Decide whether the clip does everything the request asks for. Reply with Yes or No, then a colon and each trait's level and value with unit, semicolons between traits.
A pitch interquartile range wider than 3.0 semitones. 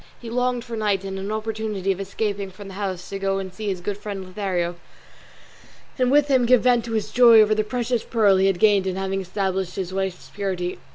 No: average, 2.7 semitones